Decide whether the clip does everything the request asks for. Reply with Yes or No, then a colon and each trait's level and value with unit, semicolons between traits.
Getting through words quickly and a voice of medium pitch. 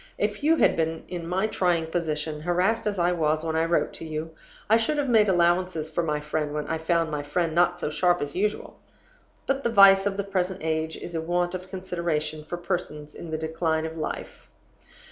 Yes: fast, 215 wpm; medium, 170 Hz